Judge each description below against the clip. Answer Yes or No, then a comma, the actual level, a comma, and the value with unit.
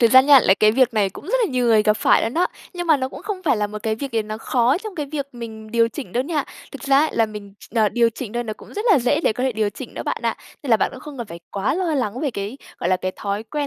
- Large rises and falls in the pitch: No, average, 4.6 semitones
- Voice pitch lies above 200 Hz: Yes, high, 240 Hz